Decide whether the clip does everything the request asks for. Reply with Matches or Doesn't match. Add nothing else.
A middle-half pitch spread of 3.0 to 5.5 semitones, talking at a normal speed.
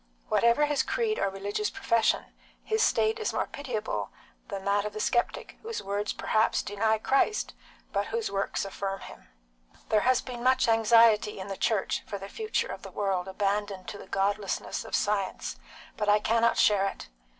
Matches